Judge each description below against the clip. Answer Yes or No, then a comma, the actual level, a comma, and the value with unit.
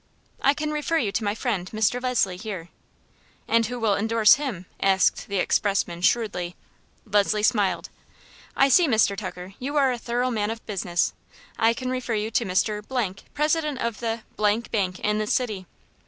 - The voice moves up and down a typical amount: Yes, average, 3.8 semitones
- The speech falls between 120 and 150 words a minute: No, average, 170 wpm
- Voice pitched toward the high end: Yes, high, 220 Hz